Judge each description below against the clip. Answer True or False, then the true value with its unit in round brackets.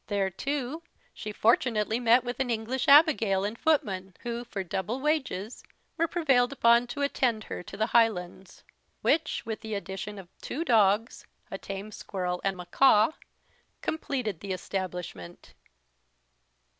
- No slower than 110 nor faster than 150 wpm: True (140 wpm)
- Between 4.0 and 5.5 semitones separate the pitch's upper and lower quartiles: True (4.6 semitones)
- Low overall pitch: False (220 Hz)